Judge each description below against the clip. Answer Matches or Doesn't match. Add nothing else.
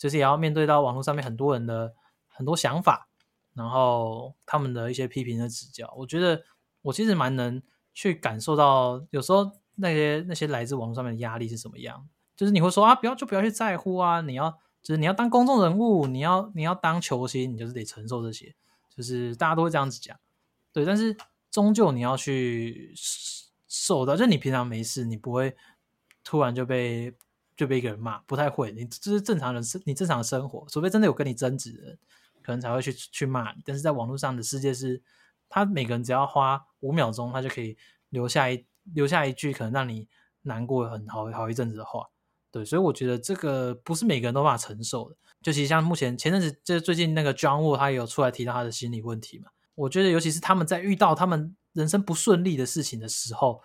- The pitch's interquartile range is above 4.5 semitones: Matches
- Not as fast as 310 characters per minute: Doesn't match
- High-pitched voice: Doesn't match